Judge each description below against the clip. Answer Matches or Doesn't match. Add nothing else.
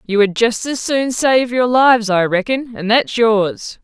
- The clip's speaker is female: Matches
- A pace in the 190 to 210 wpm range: Matches